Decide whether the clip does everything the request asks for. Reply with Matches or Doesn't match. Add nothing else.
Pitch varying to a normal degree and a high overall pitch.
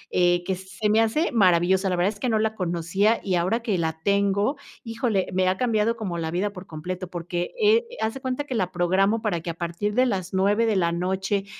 Matches